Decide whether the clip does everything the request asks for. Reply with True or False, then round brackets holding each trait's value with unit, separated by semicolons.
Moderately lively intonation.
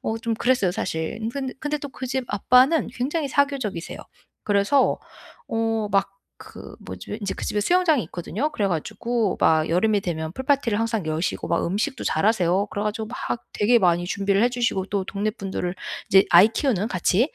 True (4.7 semitones)